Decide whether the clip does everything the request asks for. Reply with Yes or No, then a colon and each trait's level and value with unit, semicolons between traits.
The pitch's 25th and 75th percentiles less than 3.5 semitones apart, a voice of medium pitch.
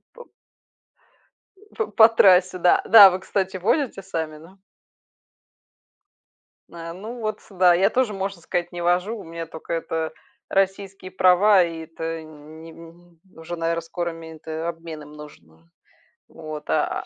Yes: average, 2.9 semitones; medium, 175 Hz